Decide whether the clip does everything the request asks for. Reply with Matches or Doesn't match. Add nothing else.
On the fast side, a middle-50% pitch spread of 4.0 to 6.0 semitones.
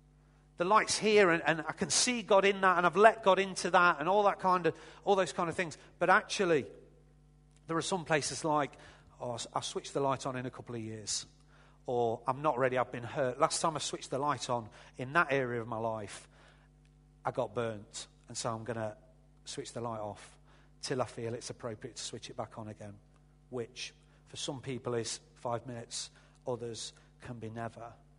Matches